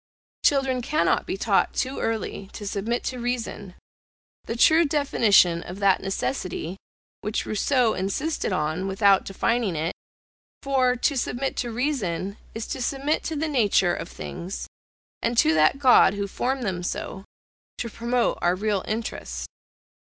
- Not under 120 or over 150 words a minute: Yes, average, 145 wpm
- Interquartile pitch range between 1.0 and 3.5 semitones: No, average, 5.1 semitones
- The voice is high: Yes, high, 225 Hz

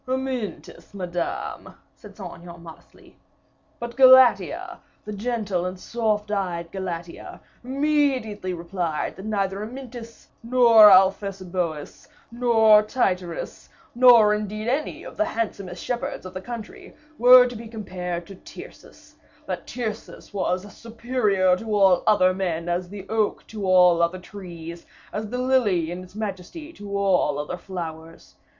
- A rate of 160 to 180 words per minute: No, slow, 135 wpm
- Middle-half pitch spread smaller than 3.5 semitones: No, average, 4.4 semitones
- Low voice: No, high, 200 Hz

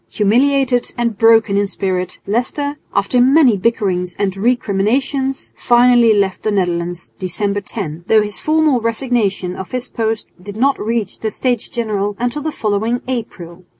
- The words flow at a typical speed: Yes, average, 150 wpm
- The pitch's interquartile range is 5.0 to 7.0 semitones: No, average, 3.9 semitones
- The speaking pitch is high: Yes, high, 220 Hz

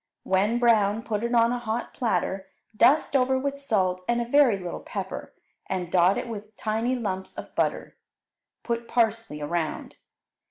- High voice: Yes, high, 225 Hz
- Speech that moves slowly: No, average, 160 wpm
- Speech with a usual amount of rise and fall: Yes, average, 4.0 semitones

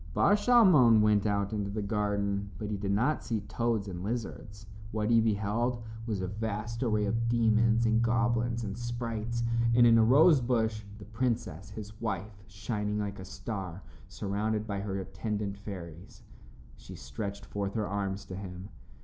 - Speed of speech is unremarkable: Yes, average, 165 wpm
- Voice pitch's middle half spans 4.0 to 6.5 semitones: No, narrow, 2.5 semitones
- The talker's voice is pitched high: No, low, 105 Hz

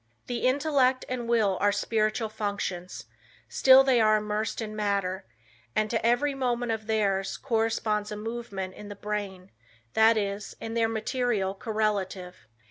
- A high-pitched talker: Yes, high, 215 Hz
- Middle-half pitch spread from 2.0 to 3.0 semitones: Yes, average, 2.7 semitones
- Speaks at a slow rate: No, average, 145 wpm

